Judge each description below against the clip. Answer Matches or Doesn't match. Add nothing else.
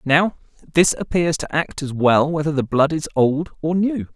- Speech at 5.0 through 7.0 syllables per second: Doesn't match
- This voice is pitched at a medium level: Matches